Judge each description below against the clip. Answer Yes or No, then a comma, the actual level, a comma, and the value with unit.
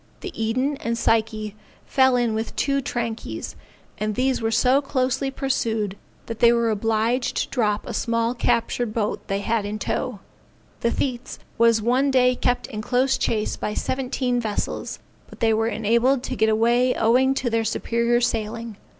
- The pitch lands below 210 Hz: No, high, 235 Hz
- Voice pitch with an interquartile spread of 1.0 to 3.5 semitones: Yes, narrow, 2.4 semitones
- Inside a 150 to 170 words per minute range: Yes, average, 165 wpm